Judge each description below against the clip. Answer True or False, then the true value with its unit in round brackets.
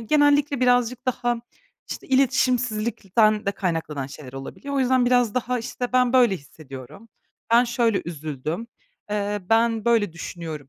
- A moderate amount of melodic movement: False (6.1 semitones)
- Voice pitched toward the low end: False (230 Hz)